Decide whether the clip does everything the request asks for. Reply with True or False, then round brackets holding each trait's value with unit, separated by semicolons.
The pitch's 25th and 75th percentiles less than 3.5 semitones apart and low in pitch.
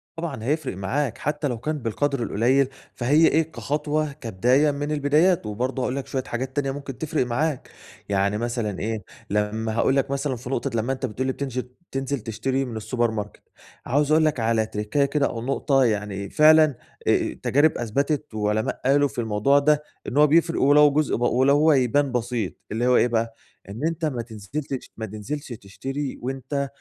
False (4.2 semitones; 130 Hz)